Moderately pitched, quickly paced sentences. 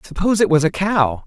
Yes: medium, 170 Hz; fast, 240 wpm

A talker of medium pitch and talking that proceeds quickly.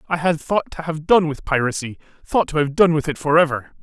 Yes: medium, 155 Hz; fast, 250 wpm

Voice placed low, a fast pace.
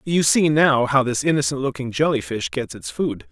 Yes: low, 130 Hz; fast, 215 wpm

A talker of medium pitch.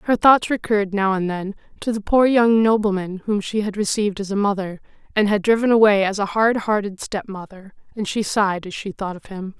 No: high, 205 Hz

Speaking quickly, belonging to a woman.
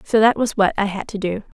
Yes: fast, 300 wpm; female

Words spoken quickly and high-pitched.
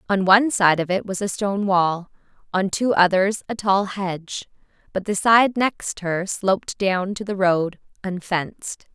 No: average, 175 wpm; high, 195 Hz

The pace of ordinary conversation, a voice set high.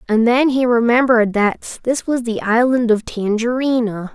Yes: average, 160 wpm; high, 235 Hz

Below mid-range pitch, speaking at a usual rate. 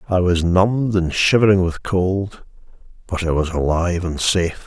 Yes: very low, 90 Hz; average, 155 wpm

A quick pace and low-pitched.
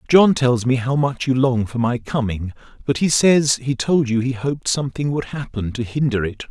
Yes: fast, 220 wpm; low, 130 Hz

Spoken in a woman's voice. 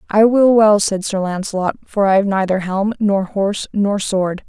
Yes: female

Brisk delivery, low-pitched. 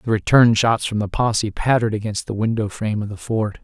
Yes: fast, 230 wpm; low, 110 Hz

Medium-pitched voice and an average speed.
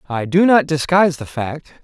Yes: medium, 150 Hz; average, 195 wpm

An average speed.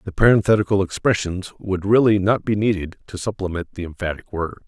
Yes: average, 165 wpm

